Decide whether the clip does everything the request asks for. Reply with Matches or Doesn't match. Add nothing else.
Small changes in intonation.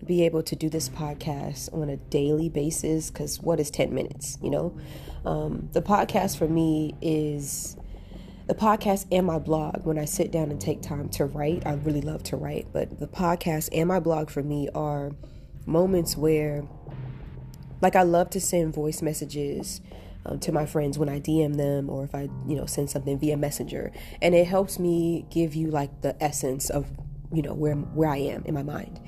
Matches